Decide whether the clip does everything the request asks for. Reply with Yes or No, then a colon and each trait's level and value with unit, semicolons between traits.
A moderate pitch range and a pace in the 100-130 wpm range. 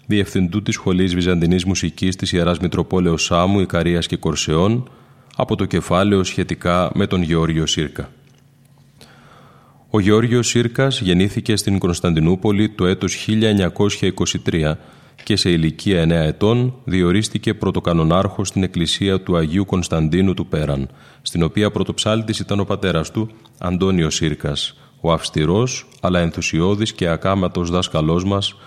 Yes: average, 3.8 semitones; average, 125 wpm